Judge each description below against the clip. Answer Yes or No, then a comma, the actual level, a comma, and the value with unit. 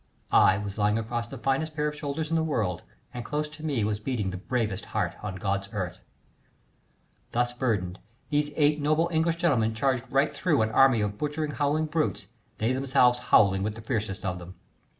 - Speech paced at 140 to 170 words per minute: No, average, 190 wpm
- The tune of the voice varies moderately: No, wide, 6.2 semitones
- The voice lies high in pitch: No, low, 120 Hz